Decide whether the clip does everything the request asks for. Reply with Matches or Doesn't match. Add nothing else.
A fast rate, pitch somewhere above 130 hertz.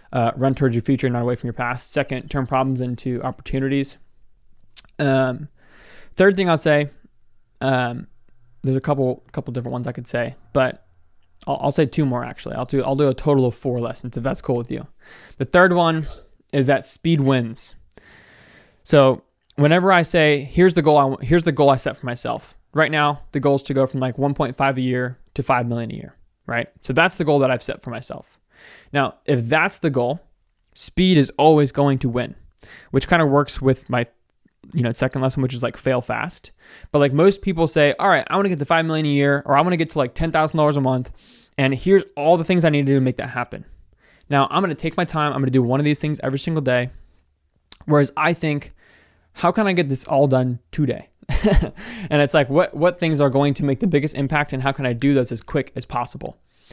Matches